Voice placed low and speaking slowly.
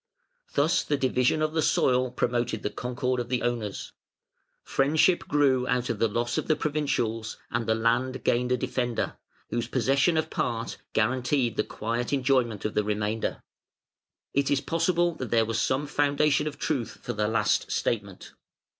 No: low, 125 Hz; average, 165 wpm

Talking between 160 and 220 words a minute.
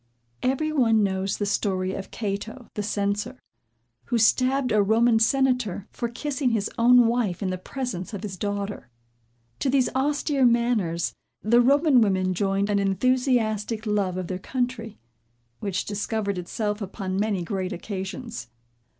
No: average, 145 wpm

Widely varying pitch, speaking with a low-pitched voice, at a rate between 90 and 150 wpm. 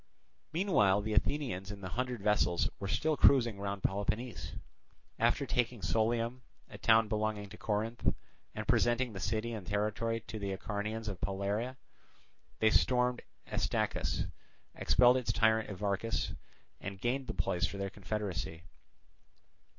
No: average, 3.1 semitones; low, 110 Hz; slow, 135 wpm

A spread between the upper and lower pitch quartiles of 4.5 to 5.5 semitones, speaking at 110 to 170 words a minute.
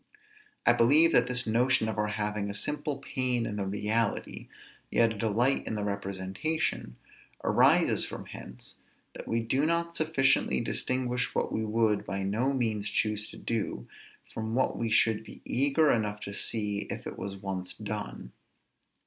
No: average, 3.7 semitones; average, 165 wpm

